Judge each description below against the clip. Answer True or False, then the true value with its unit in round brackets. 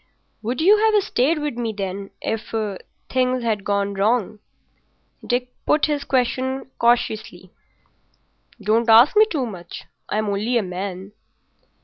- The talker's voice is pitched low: False (230 Hz)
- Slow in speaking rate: True (125 wpm)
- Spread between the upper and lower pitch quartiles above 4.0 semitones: True (4.4 semitones)